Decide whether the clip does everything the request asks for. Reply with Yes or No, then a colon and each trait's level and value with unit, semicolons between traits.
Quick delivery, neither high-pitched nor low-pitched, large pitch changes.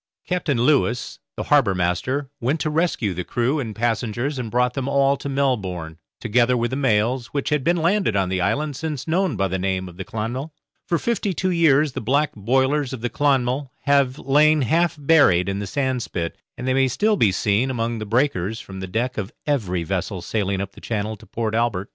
No: fast, 210 wpm; low, 125 Hz; wide, 5.7 semitones